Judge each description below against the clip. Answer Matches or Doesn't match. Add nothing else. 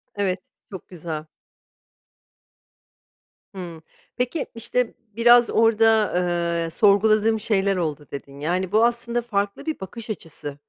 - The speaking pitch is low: Doesn't match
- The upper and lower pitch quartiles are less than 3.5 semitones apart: Doesn't match